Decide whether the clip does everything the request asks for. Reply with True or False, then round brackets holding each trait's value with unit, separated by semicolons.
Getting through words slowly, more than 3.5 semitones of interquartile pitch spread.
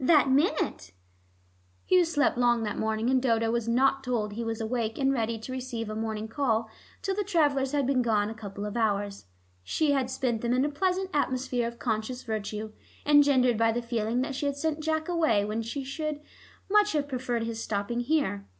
False (200 wpm; 4.2 semitones)